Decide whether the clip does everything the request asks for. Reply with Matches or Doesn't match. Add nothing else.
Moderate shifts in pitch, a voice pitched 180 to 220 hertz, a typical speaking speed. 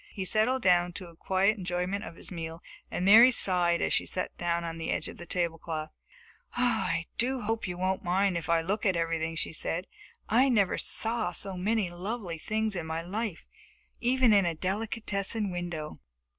Matches